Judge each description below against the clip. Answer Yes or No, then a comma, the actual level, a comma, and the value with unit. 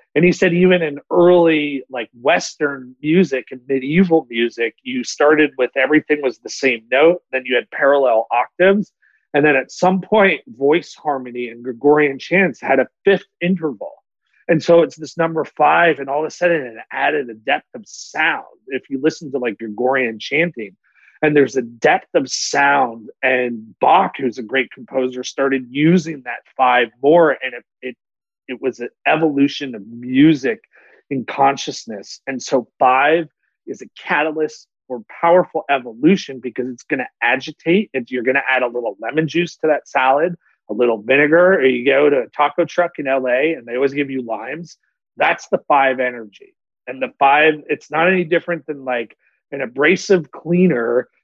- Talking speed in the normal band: Yes, average, 175 wpm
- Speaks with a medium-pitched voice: Yes, medium, 145 Hz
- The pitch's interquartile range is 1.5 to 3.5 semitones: No, average, 4.8 semitones